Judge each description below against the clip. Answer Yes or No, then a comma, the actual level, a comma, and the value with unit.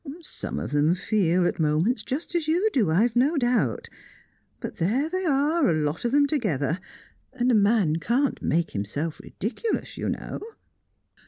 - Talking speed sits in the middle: Yes, average, 165 wpm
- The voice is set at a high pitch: Yes, high, 225 Hz